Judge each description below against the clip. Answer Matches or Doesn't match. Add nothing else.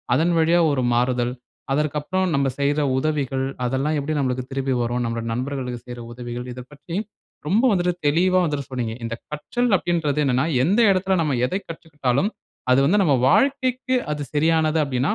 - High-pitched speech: Doesn't match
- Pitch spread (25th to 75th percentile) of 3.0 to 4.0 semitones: Doesn't match